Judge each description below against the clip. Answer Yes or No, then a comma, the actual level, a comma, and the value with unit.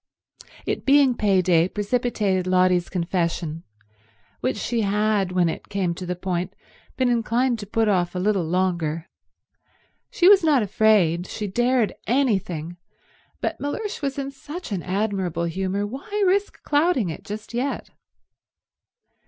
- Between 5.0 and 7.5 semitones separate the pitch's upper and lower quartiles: Yes, wide, 5.5 semitones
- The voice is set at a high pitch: Yes, high, 205 Hz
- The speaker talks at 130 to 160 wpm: Yes, slow, 135 wpm